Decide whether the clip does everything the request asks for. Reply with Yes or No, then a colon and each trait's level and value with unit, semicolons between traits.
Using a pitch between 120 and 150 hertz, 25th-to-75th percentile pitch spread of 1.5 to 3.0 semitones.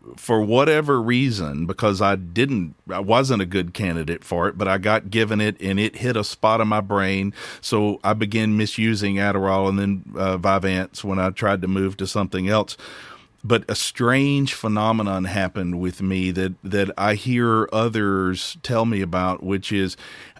No: low, 100 Hz; narrow, 2.5 semitones